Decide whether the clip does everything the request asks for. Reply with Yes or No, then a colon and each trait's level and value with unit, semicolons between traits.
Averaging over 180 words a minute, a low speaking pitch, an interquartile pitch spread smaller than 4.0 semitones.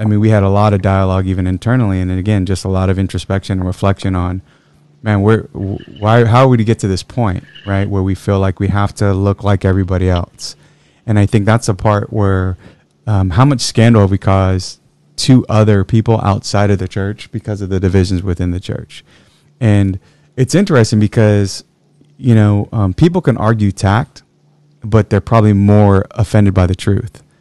Yes: average, 195 wpm; low, 100 Hz; average, 2.7 semitones